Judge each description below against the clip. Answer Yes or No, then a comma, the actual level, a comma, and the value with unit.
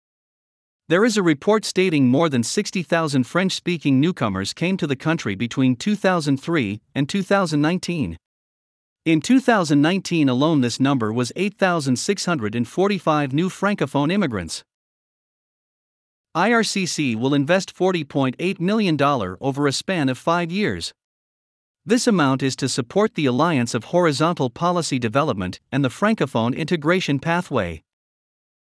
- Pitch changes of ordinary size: No, wide, 5.7 semitones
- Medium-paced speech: No, slow, 115 wpm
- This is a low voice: No, medium, 155 Hz